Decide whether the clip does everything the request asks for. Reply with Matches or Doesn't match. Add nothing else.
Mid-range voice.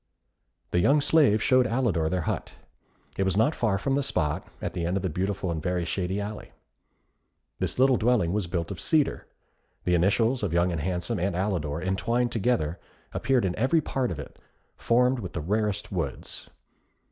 Doesn't match